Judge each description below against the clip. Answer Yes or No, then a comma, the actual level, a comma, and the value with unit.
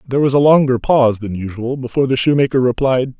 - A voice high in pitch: No, low, 130 Hz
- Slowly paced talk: No, fast, 205 wpm